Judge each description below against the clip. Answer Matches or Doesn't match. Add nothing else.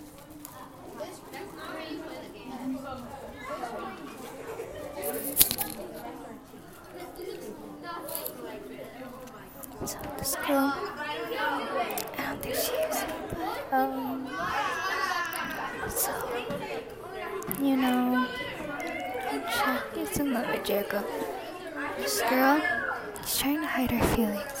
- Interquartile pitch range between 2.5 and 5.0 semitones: Doesn't match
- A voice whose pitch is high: Matches